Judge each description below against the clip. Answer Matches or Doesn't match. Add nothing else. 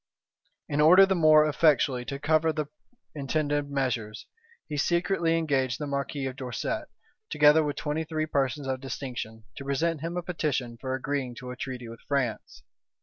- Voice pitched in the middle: Matches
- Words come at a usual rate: Matches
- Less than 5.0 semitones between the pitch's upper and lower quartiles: Matches